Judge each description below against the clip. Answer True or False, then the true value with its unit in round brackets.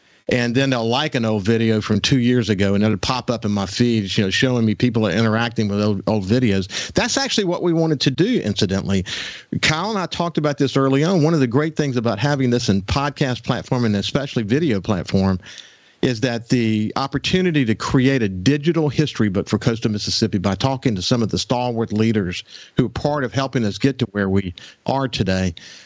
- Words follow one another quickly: True (215 wpm)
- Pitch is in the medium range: False (120 Hz)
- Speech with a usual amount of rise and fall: True (4.5 semitones)